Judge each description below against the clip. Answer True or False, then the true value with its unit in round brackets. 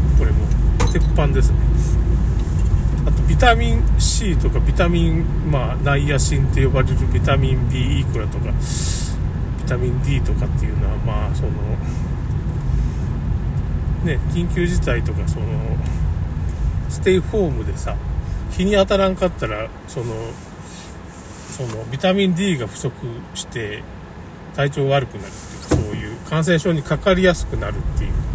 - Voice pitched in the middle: False (105 Hz)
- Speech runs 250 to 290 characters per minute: True (270 characters per minute)